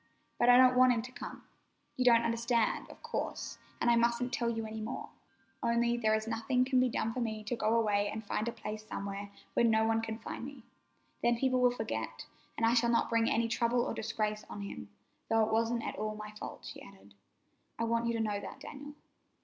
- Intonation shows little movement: Yes, narrow, 1.7 semitones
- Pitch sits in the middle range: No, high, 230 Hz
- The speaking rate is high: Yes, fast, 225 wpm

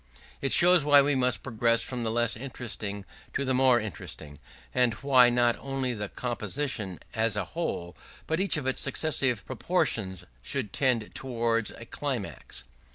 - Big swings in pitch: No, average, 3.9 semitones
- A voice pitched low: Yes, low, 120 Hz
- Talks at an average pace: Yes, average, 160 wpm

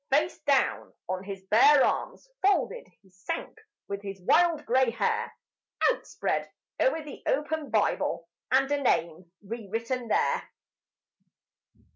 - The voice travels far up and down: Yes, wide, 7.0 semitones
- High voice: Yes, very high, 260 Hz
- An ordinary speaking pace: No, slow, 125 wpm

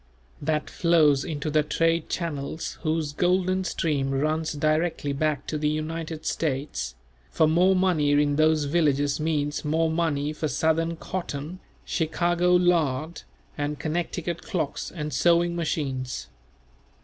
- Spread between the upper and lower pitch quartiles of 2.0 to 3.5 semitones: Yes, narrow, 2.4 semitones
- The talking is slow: Yes, slow, 125 wpm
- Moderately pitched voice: Yes, medium, 155 Hz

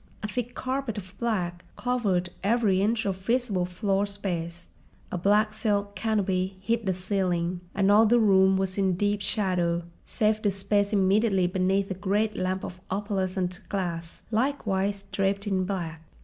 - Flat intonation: Yes, narrow, 2.3 semitones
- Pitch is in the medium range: No, high, 195 Hz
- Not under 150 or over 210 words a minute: Yes, average, 155 wpm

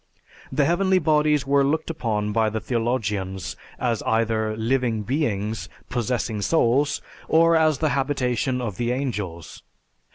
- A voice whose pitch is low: Yes, low, 125 Hz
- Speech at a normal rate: No, slow, 130 wpm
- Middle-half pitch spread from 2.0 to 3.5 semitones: No, average, 4.8 semitones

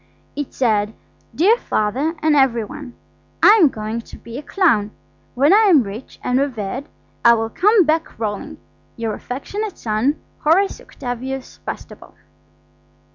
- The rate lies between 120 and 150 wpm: Yes, slow, 135 wpm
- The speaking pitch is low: No, very high, 265 Hz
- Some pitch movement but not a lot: No, wide, 5.9 semitones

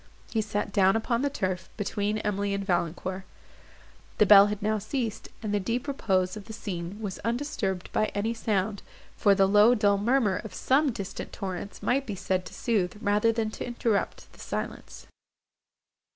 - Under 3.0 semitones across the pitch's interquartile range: Yes, narrow, 2.6 semitones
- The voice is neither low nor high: No, high, 205 Hz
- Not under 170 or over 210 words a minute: Yes, average, 175 wpm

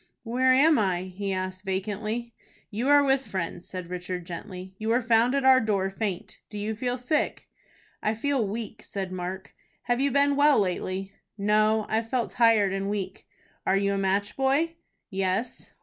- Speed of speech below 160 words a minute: No, average, 175 wpm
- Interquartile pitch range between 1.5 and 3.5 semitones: No, average, 4.5 semitones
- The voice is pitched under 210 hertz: No, high, 215 Hz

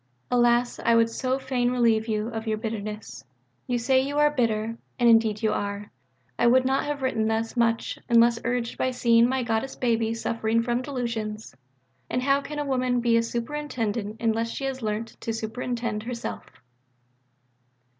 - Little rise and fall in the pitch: Yes, narrow, 2.2 semitones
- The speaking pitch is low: No, high, 235 Hz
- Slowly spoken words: No, average, 170 wpm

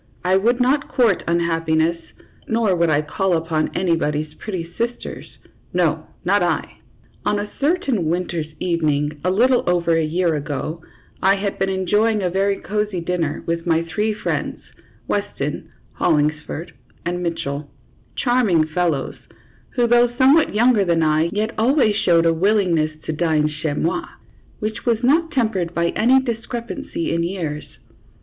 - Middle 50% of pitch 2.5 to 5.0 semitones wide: No, wide, 5.4 semitones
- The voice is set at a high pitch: No, medium, 180 Hz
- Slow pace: No, average, 145 wpm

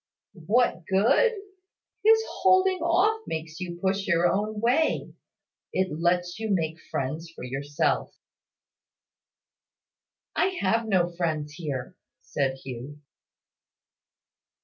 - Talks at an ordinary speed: No, slow, 105 wpm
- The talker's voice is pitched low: No, medium, 180 Hz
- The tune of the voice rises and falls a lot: Yes, wide, 6.4 semitones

